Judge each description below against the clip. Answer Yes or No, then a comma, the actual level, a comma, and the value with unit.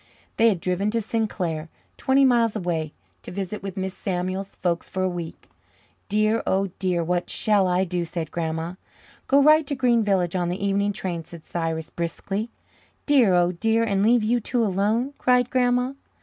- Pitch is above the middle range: Yes, high, 195 Hz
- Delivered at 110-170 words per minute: No, average, 180 wpm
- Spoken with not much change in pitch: No, average, 4.5 semitones